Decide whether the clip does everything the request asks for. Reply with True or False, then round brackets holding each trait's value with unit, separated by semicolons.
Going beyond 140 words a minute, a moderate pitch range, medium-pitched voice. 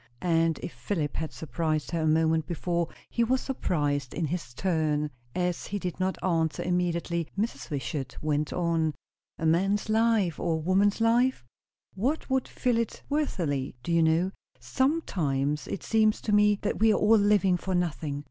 True (170 wpm; 4.8 semitones; 175 Hz)